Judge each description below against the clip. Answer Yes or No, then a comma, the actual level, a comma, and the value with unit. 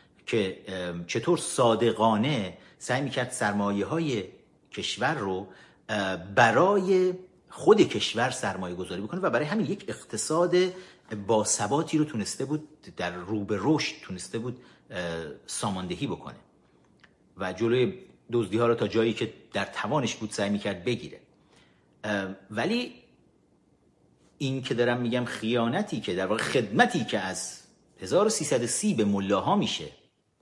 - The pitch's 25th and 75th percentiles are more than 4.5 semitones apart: Yes, average, 4.9 semitones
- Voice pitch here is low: Yes, low, 115 Hz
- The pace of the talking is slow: No, average, 120 wpm